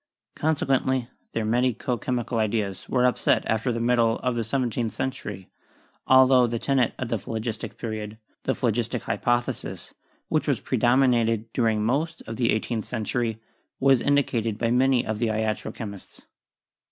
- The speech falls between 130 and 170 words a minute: Yes, average, 155 wpm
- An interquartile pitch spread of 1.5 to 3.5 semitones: Yes, narrow, 2.4 semitones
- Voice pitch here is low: Yes, low, 120 Hz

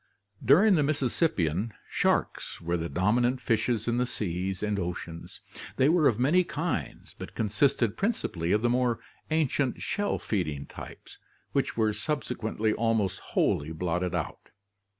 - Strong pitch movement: Yes, wide, 6.6 semitones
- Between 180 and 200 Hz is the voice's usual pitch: No, low, 110 Hz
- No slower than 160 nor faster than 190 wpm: No, average, 150 wpm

